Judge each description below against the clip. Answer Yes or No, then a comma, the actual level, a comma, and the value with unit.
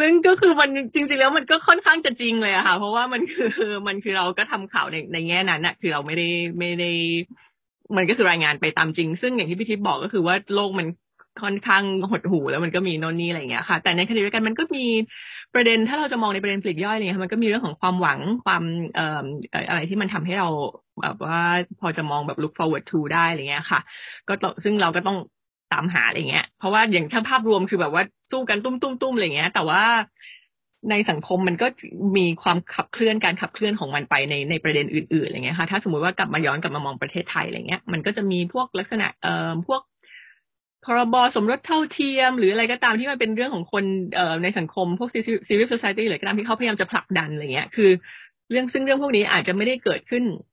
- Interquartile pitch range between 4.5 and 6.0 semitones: Yes, average, 4.8 semitones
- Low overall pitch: No, high, 195 Hz